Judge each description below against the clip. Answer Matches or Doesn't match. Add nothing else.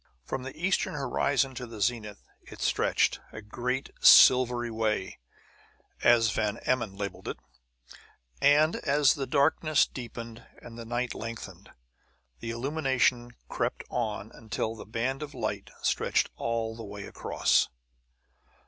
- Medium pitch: Doesn't match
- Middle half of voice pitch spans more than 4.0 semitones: Doesn't match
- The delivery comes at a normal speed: Doesn't match